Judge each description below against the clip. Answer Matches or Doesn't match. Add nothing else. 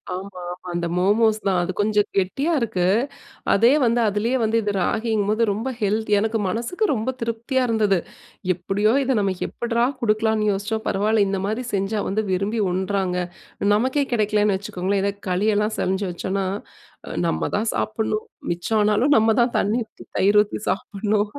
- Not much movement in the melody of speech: Matches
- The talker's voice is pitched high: Matches